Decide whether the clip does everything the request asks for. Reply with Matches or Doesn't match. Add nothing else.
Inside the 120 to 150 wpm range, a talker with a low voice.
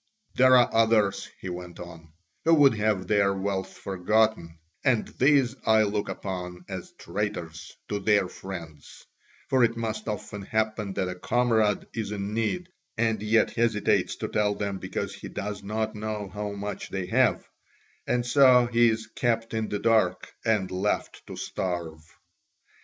Doesn't match